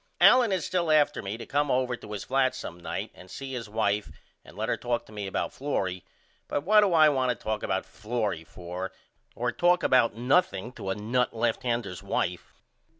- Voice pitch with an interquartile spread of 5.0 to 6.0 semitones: Yes, average, 5.3 semitones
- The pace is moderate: No, fast, 210 wpm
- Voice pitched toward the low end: Yes, low, 120 Hz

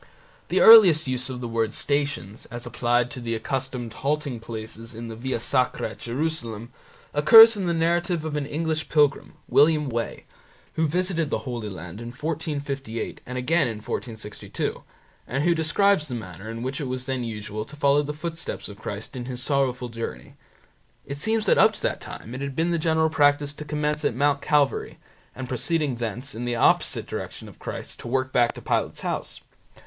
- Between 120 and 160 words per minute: No, average, 190 wpm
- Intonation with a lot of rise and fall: No, average, 4.4 semitones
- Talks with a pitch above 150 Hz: No, low, 135 Hz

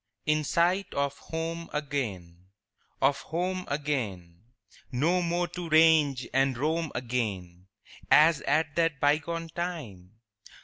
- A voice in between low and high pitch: Yes, medium, 150 Hz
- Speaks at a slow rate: Yes, slow, 115 wpm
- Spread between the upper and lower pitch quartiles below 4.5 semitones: No, average, 5.0 semitones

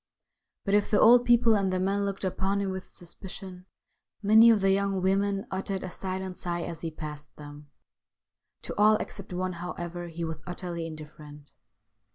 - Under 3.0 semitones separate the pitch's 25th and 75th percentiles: Yes, narrow, 2.6 semitones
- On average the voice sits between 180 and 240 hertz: Yes, medium, 185 Hz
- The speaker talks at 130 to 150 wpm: No, average, 175 wpm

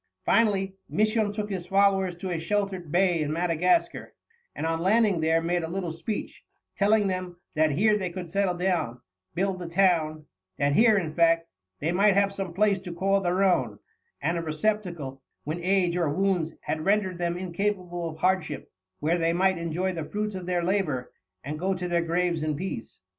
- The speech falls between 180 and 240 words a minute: Yes, average, 185 wpm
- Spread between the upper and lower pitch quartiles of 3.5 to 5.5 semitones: No, average, 2.8 semitones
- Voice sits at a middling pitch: Yes, medium, 180 Hz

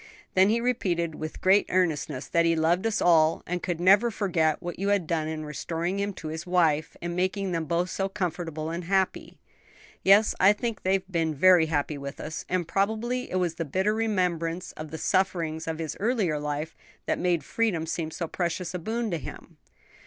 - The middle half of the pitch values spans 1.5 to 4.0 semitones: Yes, average, 3.3 semitones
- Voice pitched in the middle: Yes, medium, 175 Hz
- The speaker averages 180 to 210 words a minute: Yes, average, 195 wpm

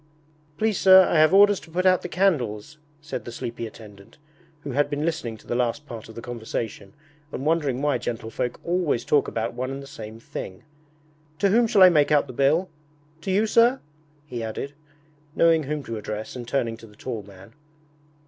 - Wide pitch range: Yes, wide, 6.6 semitones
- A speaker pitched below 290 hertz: Yes, medium, 140 Hz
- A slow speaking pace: No, average, 195 wpm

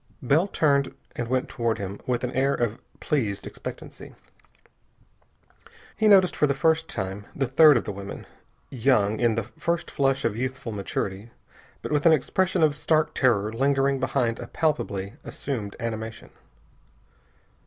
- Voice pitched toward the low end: Yes, low, 130 Hz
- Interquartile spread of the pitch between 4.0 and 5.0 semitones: Yes, average, 4.6 semitones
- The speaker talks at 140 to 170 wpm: Yes, average, 150 wpm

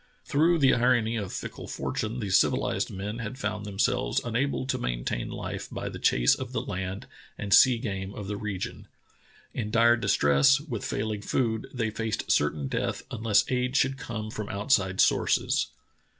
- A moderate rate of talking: Yes, average, 170 wpm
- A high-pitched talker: No, low, 110 Hz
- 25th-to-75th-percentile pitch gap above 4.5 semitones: No, average, 3.9 semitones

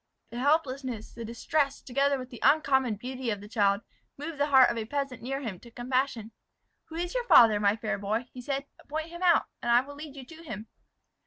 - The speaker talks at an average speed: No, fast, 220 wpm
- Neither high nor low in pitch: No, very high, 260 Hz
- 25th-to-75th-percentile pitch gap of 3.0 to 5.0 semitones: Yes, average, 3.8 semitones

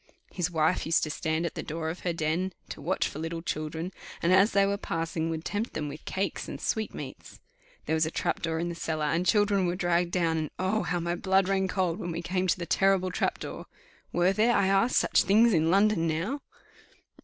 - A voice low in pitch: No, medium, 175 Hz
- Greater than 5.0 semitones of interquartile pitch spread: No, average, 3.0 semitones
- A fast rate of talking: Yes, fast, 235 wpm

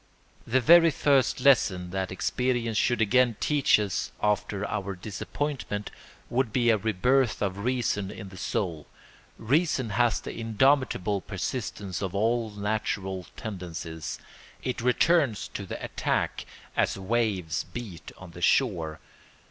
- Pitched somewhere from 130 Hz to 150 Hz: No, low, 110 Hz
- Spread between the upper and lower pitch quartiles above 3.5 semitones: Yes, average, 4.6 semitones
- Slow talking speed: Yes, slow, 130 wpm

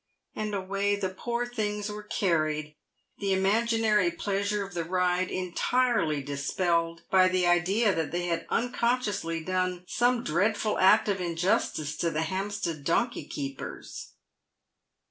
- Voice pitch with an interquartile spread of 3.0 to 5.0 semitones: Yes, average, 3.8 semitones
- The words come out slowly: Yes, slow, 130 wpm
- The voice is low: No, medium, 185 Hz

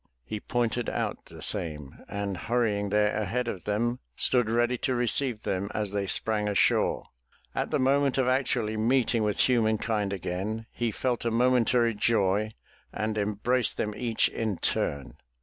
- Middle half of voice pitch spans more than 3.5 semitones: No, average, 2.8 semitones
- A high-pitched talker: No, low, 110 Hz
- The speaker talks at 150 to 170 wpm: Yes, average, 155 wpm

